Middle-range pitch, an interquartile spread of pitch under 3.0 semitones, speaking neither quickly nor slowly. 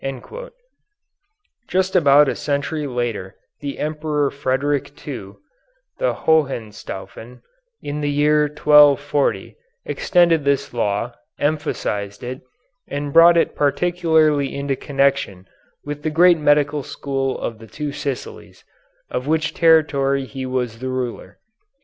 No: medium, 145 Hz; narrow, 2.6 semitones; slow, 115 wpm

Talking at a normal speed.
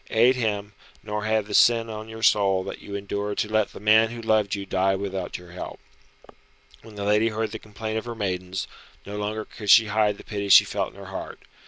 No: fast, 225 wpm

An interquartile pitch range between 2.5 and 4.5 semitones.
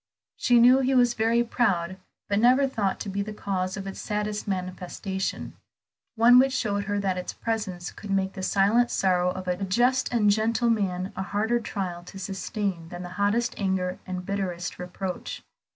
Yes: average, 3.6 semitones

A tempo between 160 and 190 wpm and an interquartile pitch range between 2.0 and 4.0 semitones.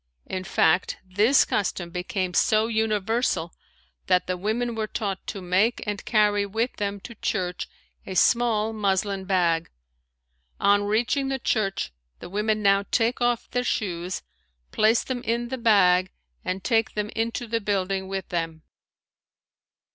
No: average, 145 wpm; average, 3.2 semitones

